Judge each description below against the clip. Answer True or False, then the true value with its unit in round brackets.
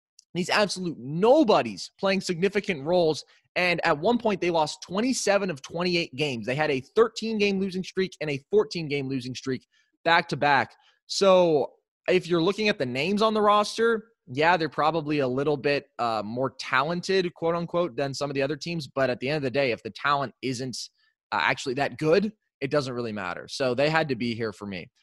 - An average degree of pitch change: False (6.1 semitones)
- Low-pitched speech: False (165 Hz)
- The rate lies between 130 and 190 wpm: False (205 wpm)